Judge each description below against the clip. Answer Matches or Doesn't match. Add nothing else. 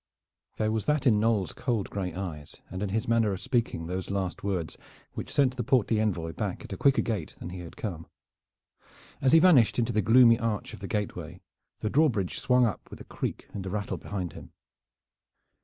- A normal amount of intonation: Matches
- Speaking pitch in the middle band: Doesn't match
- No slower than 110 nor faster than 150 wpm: Doesn't match